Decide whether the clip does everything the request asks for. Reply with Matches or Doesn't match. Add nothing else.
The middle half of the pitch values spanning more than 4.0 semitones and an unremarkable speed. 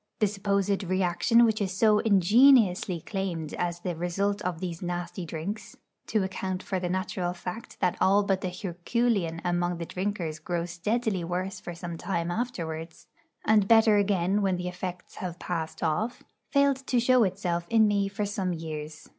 Doesn't match